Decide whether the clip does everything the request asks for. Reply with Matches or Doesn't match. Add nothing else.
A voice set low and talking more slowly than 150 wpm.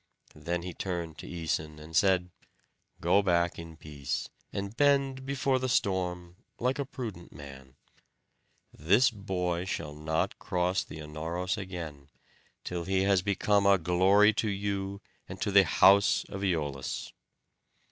Matches